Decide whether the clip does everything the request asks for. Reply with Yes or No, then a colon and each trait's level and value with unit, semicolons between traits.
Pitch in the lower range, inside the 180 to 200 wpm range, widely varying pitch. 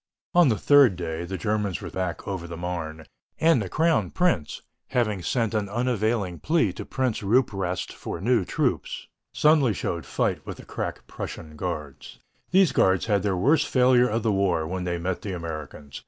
Yes: low, 100 Hz; average, 185 wpm; wide, 6.0 semitones